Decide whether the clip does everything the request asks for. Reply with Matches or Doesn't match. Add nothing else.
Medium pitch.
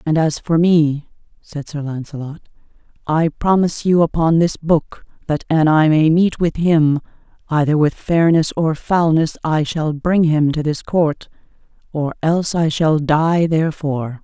Matches